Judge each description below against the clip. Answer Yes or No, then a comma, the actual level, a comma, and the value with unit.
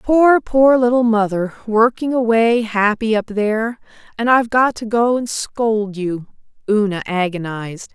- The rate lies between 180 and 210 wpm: No, average, 145 wpm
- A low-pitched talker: No, high, 220 Hz